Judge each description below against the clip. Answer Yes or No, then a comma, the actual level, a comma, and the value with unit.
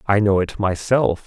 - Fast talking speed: No, average, 190 wpm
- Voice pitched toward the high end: No, low, 100 Hz